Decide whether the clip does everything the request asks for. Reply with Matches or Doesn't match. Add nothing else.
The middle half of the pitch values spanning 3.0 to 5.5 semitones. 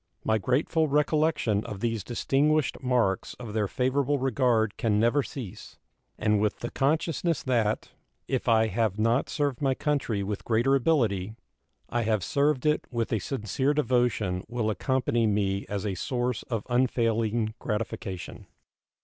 Matches